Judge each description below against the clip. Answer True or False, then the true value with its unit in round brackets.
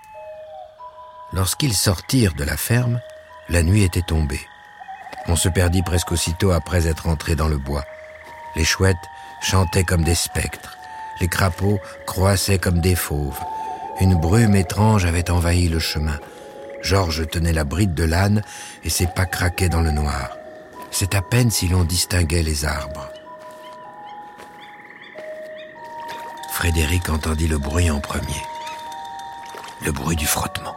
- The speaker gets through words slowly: True (135 wpm)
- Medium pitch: False (95 Hz)